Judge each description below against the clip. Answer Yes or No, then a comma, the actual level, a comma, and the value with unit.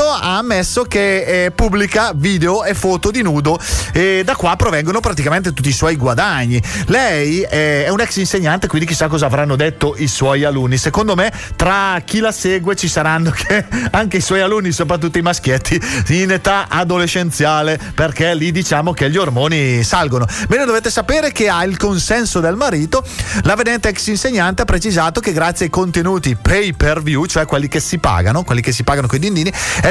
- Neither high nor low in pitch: Yes, medium, 170 Hz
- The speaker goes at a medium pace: No, fast, 185 wpm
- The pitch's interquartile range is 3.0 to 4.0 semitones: No, average, 4.7 semitones